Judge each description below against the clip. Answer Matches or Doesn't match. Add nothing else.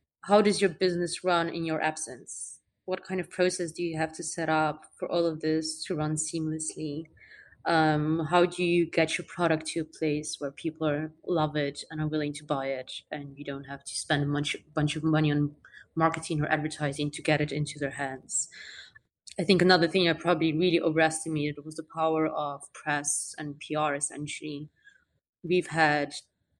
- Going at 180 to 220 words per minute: Matches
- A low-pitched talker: Doesn't match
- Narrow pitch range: Matches